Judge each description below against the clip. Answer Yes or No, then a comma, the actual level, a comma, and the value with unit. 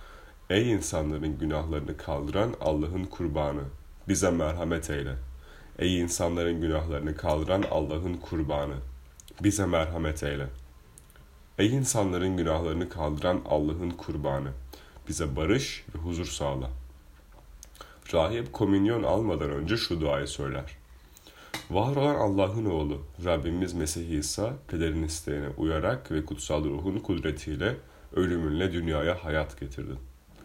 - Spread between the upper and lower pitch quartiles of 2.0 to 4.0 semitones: Yes, average, 3.7 semitones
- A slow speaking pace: No, average, 105 wpm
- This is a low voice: Yes, very low, 80 Hz